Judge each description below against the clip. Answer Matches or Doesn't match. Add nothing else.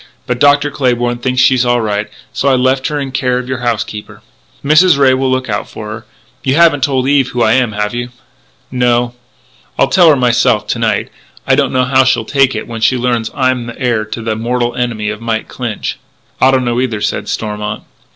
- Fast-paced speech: Matches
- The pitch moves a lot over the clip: Doesn't match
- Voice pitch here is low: Matches